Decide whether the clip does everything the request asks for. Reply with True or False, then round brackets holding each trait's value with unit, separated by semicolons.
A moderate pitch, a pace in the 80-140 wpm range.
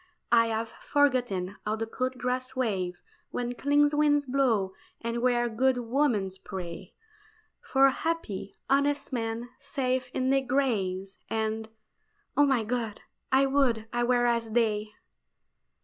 False (240 Hz; 135 wpm)